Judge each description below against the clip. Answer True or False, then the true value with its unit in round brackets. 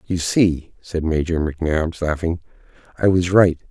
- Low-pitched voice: True (85 Hz)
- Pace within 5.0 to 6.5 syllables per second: False (4.4 syllables/s)